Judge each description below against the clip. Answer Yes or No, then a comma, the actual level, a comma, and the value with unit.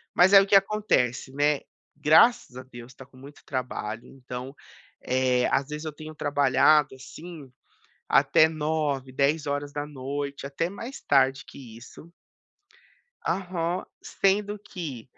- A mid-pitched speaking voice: Yes, medium, 145 Hz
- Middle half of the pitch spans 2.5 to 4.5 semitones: Yes, average, 3.6 semitones